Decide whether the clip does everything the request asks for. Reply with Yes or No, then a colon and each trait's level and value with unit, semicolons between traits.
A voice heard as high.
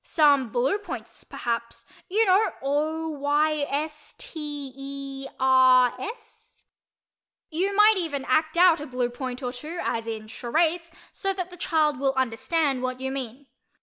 Yes: very high, 290 Hz